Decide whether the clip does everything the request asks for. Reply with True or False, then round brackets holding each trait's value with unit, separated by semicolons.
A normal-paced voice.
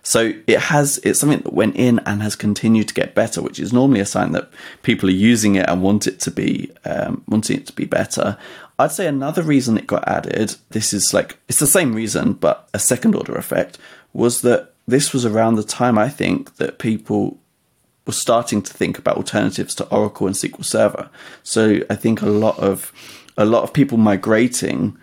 False (210 wpm)